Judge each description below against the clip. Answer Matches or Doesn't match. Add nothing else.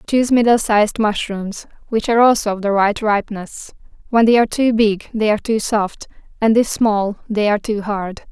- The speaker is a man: Doesn't match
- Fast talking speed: Doesn't match